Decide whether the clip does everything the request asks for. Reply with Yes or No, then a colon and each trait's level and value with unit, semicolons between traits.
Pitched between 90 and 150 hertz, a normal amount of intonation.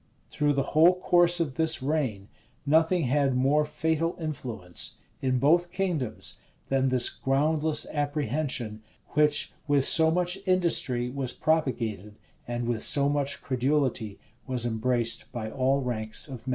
Yes: medium, 140 Hz; average, 4.3 semitones